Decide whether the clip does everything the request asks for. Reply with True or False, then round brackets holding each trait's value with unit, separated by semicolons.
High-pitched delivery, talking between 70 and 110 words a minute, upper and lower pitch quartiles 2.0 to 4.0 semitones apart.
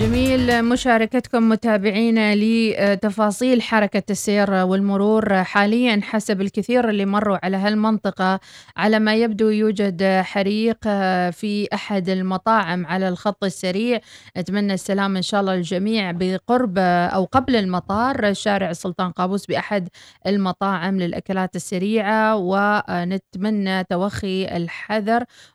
True (200 Hz; 105 wpm; 2.5 semitones)